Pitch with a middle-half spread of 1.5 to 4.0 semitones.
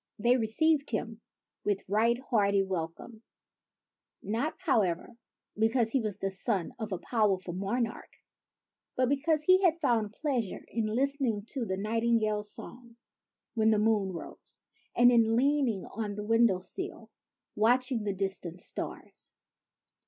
Yes: average, 3.4 semitones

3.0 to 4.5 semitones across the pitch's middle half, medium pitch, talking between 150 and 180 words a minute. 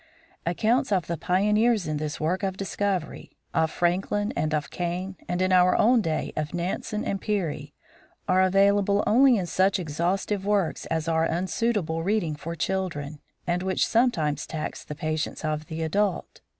Yes: average, 4.0 semitones; medium, 180 Hz; average, 165 wpm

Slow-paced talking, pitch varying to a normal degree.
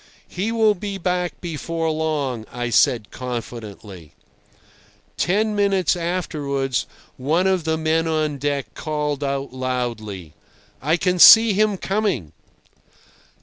No: slow, 115 wpm; wide, 6.2 semitones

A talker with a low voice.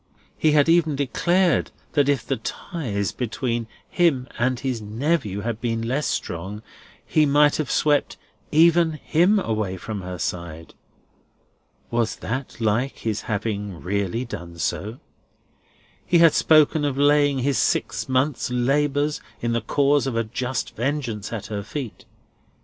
Yes: low, 125 Hz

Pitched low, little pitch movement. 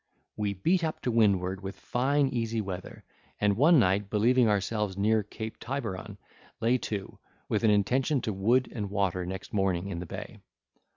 No: low, 105 Hz; average, 3.7 semitones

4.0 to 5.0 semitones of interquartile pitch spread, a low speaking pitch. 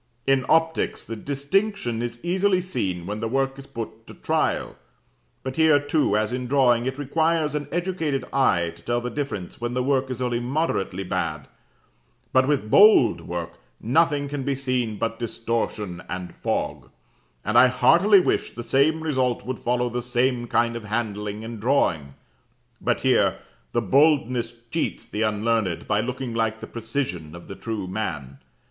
Yes: average, 4.5 semitones; low, 120 Hz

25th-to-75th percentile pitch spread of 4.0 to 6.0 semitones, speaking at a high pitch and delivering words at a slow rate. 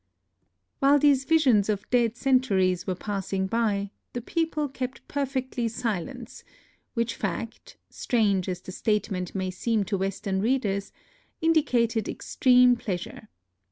Yes: average, 4.8 semitones; high, 225 Hz; slow, 130 wpm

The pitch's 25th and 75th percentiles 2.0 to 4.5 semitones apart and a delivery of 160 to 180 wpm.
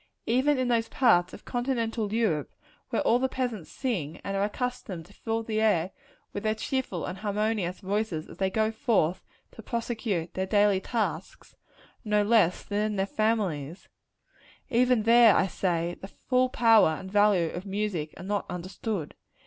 Yes: average, 3.6 semitones; average, 165 wpm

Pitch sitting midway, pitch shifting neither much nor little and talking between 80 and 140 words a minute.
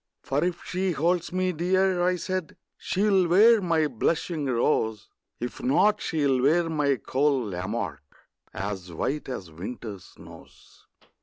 No: medium, 155 Hz; wide, 7.4 semitones; slow, 135 wpm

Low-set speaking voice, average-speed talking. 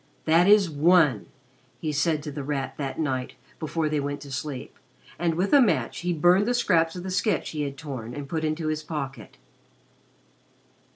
No: medium, 155 Hz; average, 185 wpm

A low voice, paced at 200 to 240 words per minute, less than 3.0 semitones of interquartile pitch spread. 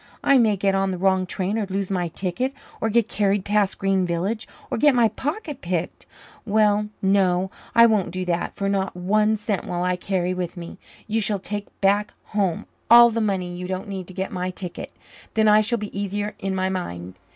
No: high, 195 Hz; fast, 205 wpm; narrow, 2.5 semitones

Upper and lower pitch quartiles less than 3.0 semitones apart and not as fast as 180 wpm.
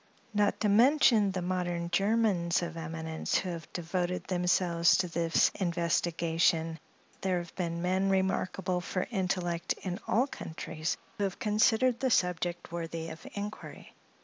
Yes: narrow, 2.5 semitones; average, 140 wpm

